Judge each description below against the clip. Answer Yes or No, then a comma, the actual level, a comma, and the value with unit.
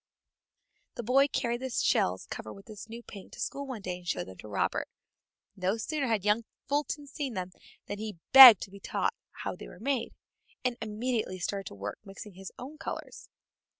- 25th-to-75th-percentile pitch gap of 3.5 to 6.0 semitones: Yes, average, 5.1 semitones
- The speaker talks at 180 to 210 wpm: Yes, average, 195 wpm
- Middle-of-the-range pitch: No, high, 215 Hz